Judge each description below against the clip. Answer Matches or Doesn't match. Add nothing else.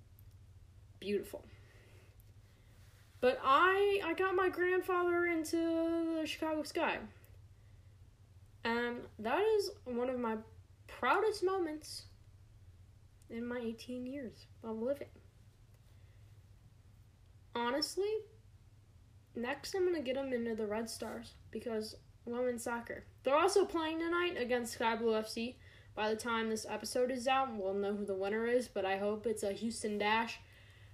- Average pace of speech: Doesn't match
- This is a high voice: Matches